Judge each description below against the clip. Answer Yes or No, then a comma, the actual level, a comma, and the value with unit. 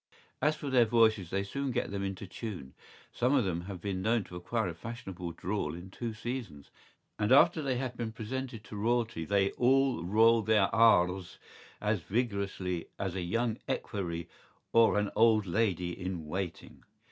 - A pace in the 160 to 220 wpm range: Yes, average, 175 wpm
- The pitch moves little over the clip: No, average, 4.2 semitones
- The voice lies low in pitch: Yes, low, 105 Hz